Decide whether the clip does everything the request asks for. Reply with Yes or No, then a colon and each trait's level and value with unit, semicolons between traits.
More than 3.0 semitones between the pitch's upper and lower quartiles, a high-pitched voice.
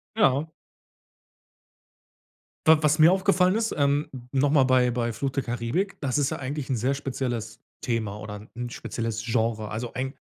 No: average, 3.9 semitones; low, 130 Hz